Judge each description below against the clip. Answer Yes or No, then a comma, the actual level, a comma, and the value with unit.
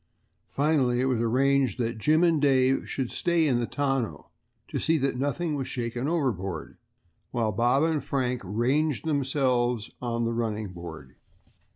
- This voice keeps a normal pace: Yes, average, 155 wpm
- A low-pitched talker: Yes, low, 130 Hz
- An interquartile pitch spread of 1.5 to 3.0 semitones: No, average, 3.4 semitones